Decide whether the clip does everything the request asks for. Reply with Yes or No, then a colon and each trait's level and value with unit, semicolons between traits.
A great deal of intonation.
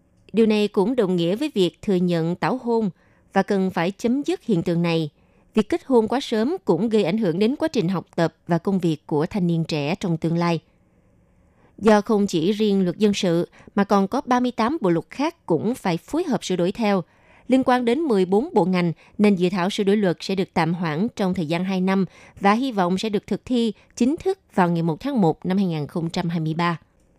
No: average, 4.2 semitones